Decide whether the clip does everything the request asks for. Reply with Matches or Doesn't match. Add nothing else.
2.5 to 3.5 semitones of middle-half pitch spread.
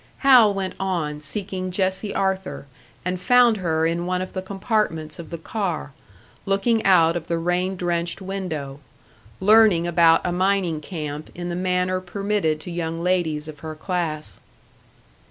Matches